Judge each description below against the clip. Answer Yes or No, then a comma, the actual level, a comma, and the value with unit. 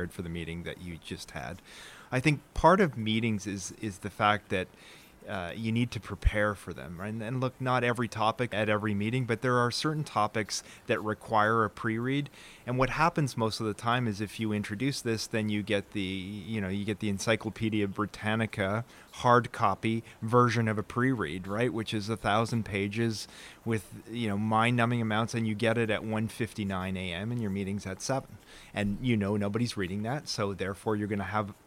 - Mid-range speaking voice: No, low, 110 Hz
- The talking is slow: No, fast, 205 wpm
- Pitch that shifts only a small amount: Yes, narrow, 2.3 semitones